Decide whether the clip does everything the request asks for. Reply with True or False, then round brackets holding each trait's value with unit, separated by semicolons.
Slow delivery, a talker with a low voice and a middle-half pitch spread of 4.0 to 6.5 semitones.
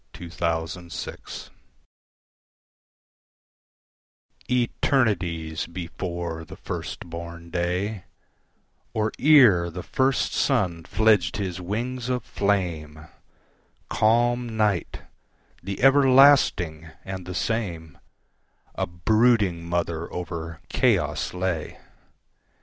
True (75 wpm; 90 Hz; 4.7 semitones)